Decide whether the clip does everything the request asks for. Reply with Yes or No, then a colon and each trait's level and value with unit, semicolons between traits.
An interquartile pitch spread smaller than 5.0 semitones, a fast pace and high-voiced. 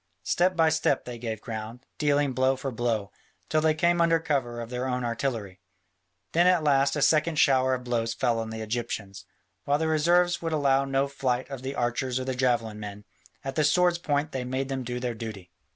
No: average, 4.1 semitones; fast, 210 wpm; low, 130 Hz